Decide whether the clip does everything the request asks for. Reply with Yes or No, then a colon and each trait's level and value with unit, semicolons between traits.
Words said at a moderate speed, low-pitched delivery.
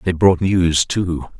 Yes: average, 170 wpm; very low, 85 Hz